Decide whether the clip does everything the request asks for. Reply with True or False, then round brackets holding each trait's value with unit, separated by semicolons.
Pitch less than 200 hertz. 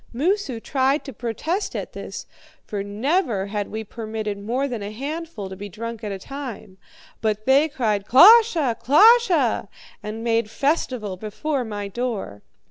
False (230 Hz)